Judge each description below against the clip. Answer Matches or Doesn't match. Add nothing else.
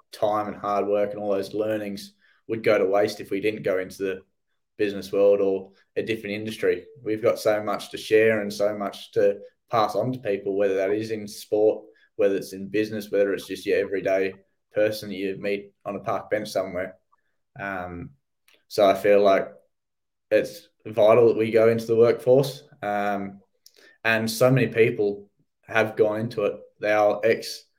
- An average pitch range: Doesn't match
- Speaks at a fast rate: Doesn't match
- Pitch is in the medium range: Doesn't match